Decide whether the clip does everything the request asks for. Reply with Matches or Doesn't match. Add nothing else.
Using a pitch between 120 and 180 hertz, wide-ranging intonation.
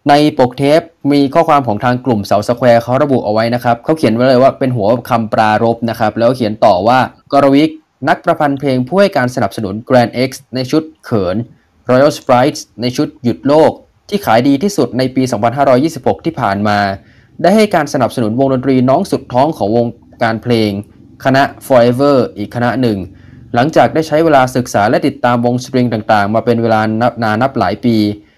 Doesn't match